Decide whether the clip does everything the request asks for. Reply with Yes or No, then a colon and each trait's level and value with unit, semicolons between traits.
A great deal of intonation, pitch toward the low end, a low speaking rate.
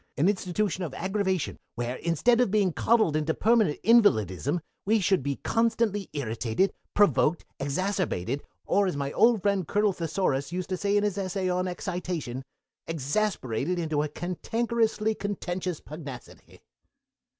No: wide, 5.7 semitones; medium, 185 Hz; slow, 130 wpm